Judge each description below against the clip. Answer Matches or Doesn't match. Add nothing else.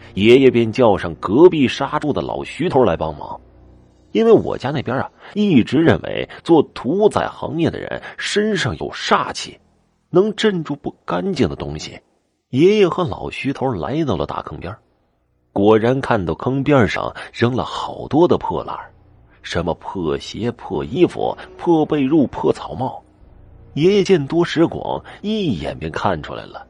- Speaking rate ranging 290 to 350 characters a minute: Doesn't match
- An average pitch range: Doesn't match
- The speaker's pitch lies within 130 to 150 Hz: Matches